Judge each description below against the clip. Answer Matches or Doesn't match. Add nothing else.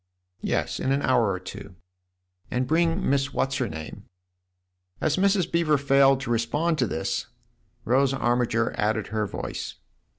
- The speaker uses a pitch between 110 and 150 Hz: Matches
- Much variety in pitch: Doesn't match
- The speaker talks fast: Doesn't match